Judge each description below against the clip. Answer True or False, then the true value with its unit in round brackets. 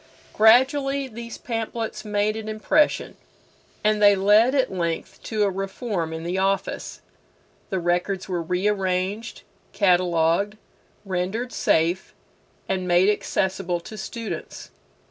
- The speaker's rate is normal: False (115 wpm)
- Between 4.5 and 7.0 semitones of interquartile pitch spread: False (3.4 semitones)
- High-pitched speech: True (195 Hz)